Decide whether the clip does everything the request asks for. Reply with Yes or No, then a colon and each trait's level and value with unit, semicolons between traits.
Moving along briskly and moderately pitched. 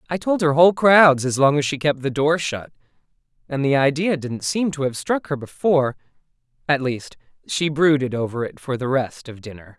Yes: fast, 210 wpm; medium, 145 Hz